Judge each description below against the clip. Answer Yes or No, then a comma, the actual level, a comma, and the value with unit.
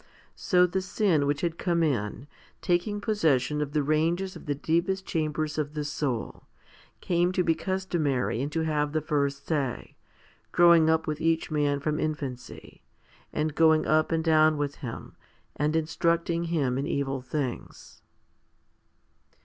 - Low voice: No, medium, 155 Hz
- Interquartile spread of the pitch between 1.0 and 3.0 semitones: Yes, average, 2.7 semitones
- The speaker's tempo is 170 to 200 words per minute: No, average, 150 wpm